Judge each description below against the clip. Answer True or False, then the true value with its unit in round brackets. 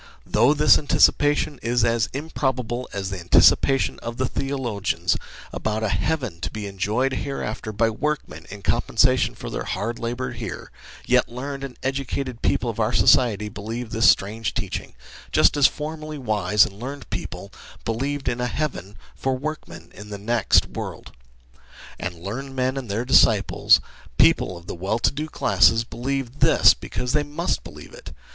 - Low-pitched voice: True (120 Hz)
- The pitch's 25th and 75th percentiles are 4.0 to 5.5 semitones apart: True (4.4 semitones)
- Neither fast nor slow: True (165 wpm)